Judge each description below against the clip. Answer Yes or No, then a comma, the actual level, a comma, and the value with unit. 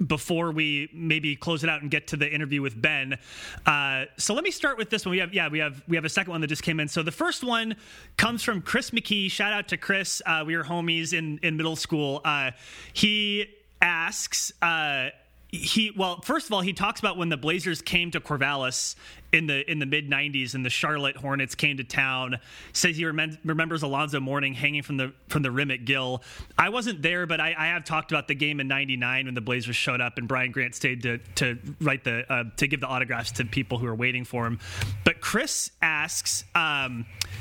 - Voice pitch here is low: No, medium, 150 Hz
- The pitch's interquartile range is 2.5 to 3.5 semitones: No, average, 4.6 semitones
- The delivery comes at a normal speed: No, fast, 230 wpm